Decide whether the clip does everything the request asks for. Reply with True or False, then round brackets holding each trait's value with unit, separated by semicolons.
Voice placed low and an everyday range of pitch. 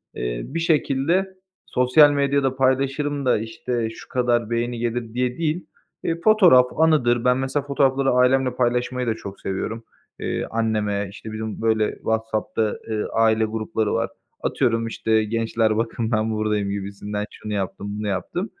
True (115 Hz; 3.4 semitones)